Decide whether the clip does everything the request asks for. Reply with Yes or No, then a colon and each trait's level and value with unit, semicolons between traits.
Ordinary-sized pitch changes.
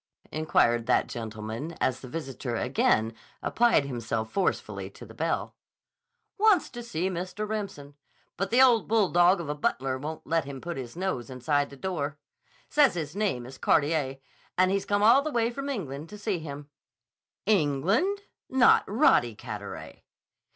No: wide, 7.8 semitones